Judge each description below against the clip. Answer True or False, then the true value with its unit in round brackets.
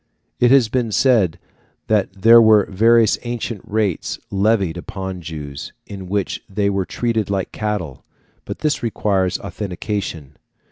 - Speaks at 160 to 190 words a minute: False (135 wpm)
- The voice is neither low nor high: False (100 Hz)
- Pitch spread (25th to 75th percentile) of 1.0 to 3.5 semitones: True (3.1 semitones)